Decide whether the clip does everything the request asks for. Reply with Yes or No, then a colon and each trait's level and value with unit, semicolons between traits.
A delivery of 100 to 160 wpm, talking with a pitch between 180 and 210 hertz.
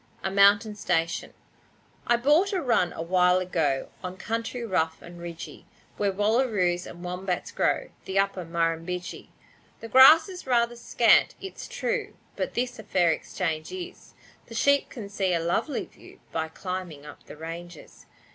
Yes: average, 155 wpm; high, 190 Hz